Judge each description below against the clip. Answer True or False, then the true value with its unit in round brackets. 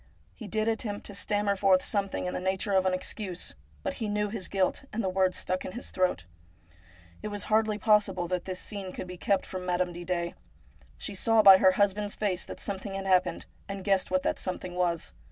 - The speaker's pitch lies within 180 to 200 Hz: True (190 Hz)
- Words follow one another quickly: True (215 wpm)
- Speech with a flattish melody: True (2.1 semitones)